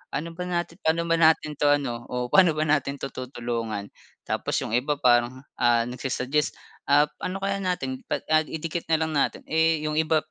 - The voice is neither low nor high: Yes, medium, 150 Hz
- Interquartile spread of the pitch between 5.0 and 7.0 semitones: No, average, 4.3 semitones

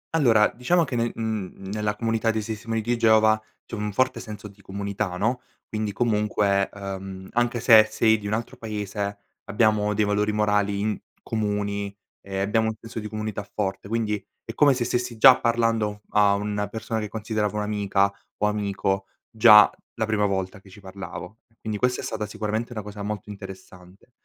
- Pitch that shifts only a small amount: Yes, narrow, 1.7 semitones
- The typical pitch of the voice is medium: No, low, 105 Hz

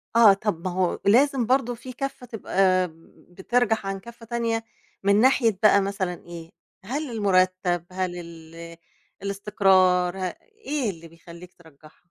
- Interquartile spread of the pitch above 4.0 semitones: Yes, average, 4.5 semitones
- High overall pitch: Yes, high, 195 Hz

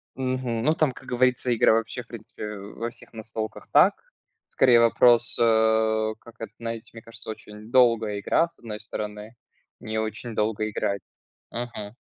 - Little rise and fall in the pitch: Yes, narrow, 2.0 semitones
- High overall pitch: No, low, 115 Hz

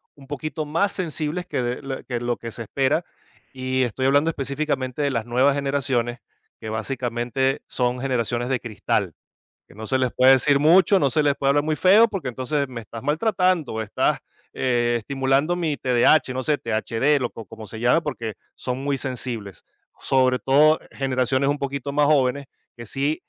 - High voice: No, low, 135 Hz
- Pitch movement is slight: No, average, 3.2 semitones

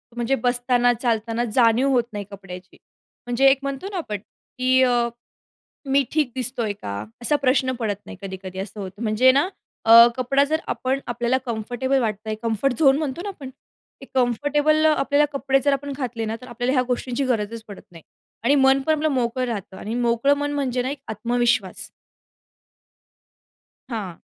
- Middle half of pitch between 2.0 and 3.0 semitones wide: No, average, 3.4 semitones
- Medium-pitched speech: No, very high, 250 Hz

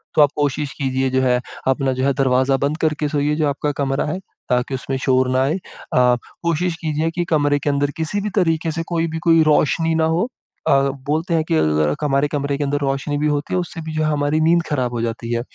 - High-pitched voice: No, medium, 145 Hz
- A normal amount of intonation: Yes, average, 3.1 semitones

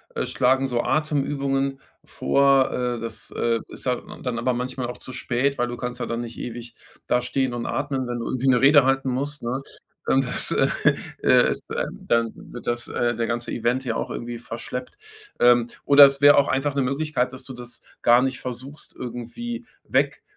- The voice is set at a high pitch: No, low, 125 Hz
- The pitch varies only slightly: Yes, narrow, 2.1 semitones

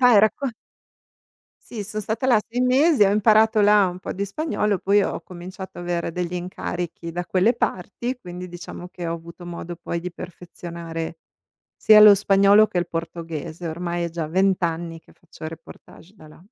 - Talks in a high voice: No, medium, 180 Hz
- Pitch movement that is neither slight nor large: Yes, average, 3.6 semitones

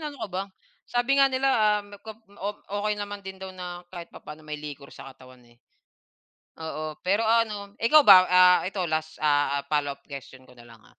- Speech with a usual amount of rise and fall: No, wide, 5.7 semitones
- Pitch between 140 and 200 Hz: Yes, medium, 185 Hz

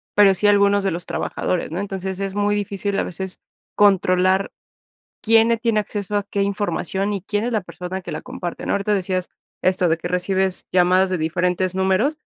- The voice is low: No, high, 190 Hz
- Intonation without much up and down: Yes, narrow, 1.9 semitones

